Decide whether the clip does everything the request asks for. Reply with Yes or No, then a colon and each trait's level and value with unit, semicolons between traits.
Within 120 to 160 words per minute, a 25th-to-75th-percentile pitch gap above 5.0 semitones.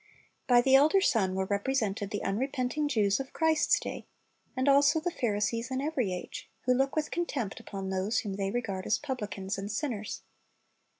No: average, 175 wpm; wide, 5.4 semitones